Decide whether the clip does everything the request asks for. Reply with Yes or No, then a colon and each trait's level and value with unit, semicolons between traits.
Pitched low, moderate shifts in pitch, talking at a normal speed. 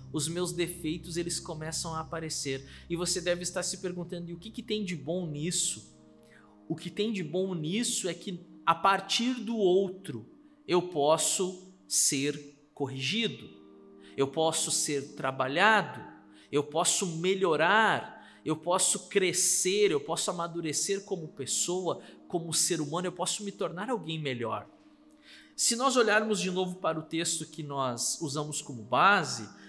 No: medium, 170 Hz; average, 4.4 semitones; average, 150 wpm